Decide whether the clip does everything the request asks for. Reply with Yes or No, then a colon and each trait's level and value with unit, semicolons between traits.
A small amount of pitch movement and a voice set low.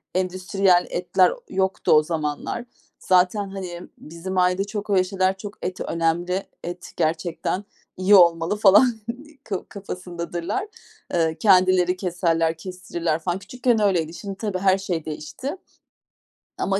No: narrow, 2.3 semitones; medium, 185 Hz